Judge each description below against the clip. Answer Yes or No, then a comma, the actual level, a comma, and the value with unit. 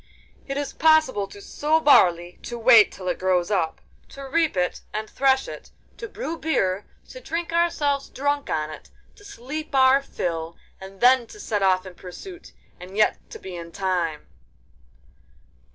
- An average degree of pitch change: No, wide, 8.2 semitones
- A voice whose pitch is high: Yes, high, 235 Hz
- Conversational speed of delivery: Yes, average, 165 wpm